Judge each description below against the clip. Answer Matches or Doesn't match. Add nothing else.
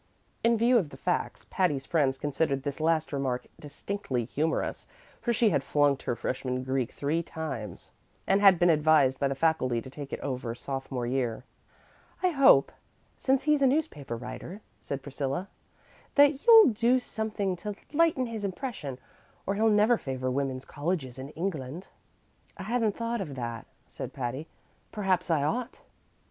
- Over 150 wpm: Matches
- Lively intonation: Matches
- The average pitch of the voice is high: Doesn't match